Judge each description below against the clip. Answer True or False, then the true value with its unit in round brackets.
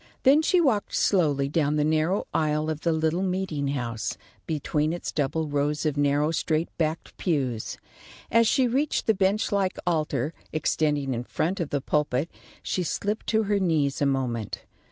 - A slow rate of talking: False (170 wpm)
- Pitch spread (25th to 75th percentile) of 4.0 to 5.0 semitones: True (4.6 semitones)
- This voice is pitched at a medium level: True (155 Hz)